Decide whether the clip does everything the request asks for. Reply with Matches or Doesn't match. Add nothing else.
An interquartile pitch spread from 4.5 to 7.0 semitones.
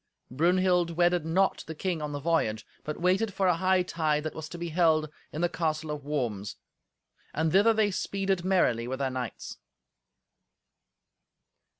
Doesn't match